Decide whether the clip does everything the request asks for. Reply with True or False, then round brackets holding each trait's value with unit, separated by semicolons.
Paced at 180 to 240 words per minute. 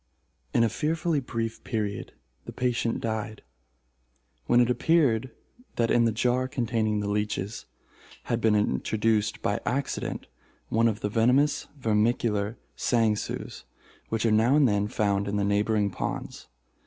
False (140 wpm)